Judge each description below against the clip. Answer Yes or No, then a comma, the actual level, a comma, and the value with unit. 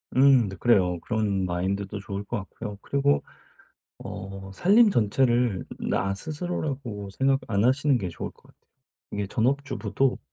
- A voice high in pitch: No, low, 110 Hz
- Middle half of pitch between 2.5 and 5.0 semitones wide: No, wide, 5.6 semitones